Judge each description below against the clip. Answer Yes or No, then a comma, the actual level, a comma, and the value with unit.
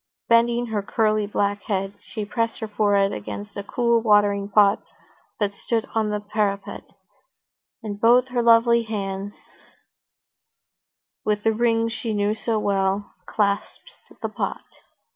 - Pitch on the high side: Yes, high, 210 Hz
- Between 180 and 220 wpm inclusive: No, slow, 135 wpm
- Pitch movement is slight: Yes, narrow, 2.1 semitones